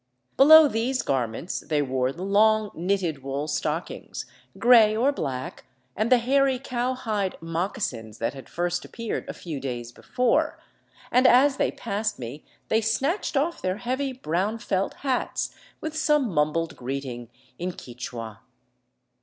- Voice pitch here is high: Yes, high, 195 Hz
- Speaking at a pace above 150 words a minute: No, average, 145 wpm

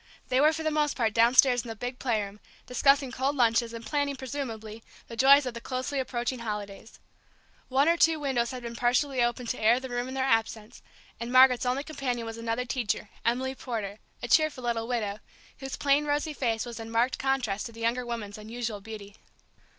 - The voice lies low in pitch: No, high, 245 Hz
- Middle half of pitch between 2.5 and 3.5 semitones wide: Yes, average, 2.8 semitones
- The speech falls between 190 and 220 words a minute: Yes, average, 200 wpm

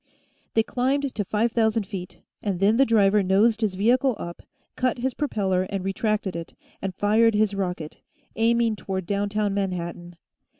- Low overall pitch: No, high, 205 Hz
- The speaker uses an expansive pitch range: No, average, 3.1 semitones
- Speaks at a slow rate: No, average, 160 wpm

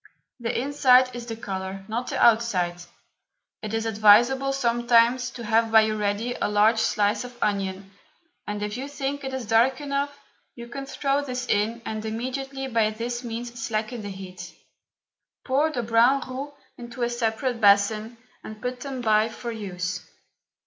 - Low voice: No, high, 230 Hz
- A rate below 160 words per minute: No, average, 165 wpm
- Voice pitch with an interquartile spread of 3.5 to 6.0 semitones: No, average, 3.0 semitones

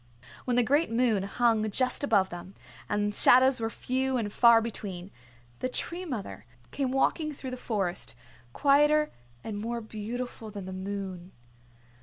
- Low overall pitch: No, high, 230 Hz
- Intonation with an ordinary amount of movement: Yes, average, 4.3 semitones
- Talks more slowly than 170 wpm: Yes, average, 150 wpm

